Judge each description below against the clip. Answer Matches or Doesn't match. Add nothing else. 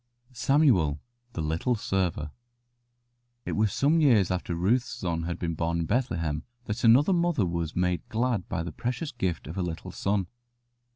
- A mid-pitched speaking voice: Doesn't match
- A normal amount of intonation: Doesn't match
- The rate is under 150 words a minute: Doesn't match